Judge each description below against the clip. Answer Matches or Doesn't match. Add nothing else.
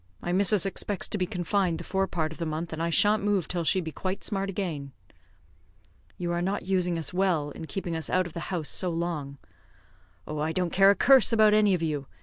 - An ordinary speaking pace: Doesn't match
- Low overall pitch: Doesn't match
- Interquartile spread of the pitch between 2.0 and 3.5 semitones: Matches